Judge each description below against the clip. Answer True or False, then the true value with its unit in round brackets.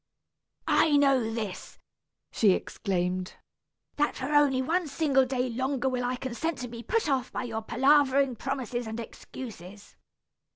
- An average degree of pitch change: True (3.4 semitones)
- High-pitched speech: True (255 Hz)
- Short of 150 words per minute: True (140 wpm)